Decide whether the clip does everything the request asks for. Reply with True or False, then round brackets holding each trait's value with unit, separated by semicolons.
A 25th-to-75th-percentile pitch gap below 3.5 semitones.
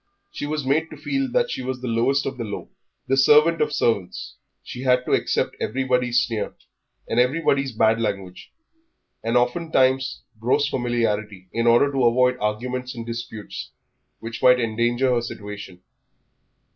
True (2.6 semitones)